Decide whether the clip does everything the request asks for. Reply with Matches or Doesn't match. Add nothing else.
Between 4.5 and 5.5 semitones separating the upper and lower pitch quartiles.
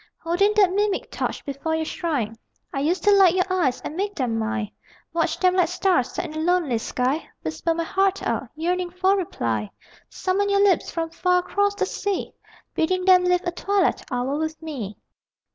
Matches